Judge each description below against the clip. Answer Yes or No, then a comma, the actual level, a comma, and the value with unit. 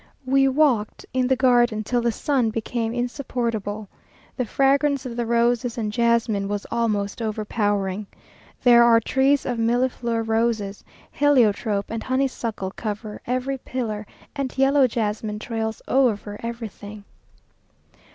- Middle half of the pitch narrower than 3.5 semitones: Yes, average, 3.0 semitones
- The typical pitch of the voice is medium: No, high, 235 Hz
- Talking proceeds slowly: Yes, slow, 125 wpm